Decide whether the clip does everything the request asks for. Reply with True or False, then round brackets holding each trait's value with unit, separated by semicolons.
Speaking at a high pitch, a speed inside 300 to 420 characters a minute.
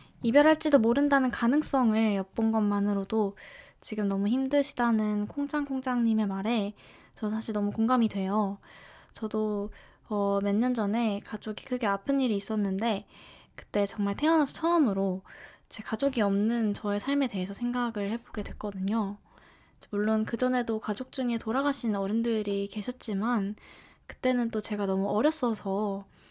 True (220 Hz; 310 characters per minute)